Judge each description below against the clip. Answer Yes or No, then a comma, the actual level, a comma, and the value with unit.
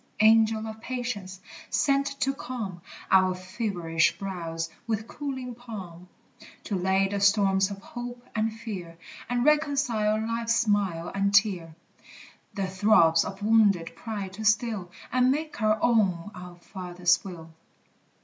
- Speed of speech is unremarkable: No, slow, 130 wpm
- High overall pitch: Yes, high, 205 Hz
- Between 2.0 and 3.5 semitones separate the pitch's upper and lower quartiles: No, average, 3.9 semitones